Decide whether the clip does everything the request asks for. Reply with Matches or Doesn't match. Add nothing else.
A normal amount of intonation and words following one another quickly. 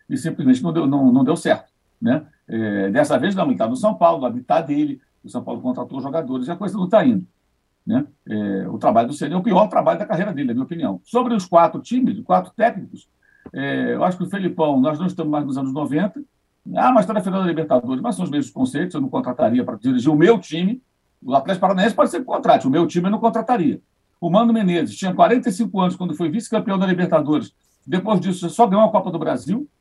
Doesn't match